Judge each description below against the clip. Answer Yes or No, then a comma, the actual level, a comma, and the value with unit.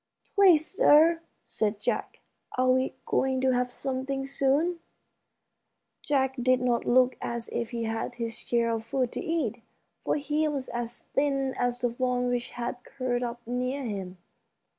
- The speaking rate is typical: Yes, average, 160 wpm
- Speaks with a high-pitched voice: Yes, very high, 255 Hz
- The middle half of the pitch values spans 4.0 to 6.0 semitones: No, narrow, 2.4 semitones